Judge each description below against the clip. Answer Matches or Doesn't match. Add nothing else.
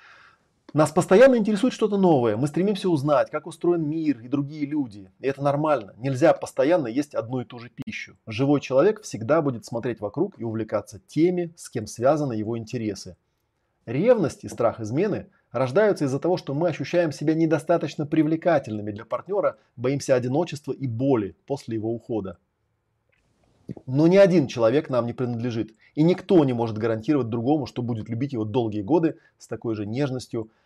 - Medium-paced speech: Doesn't match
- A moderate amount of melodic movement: Doesn't match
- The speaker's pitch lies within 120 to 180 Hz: Matches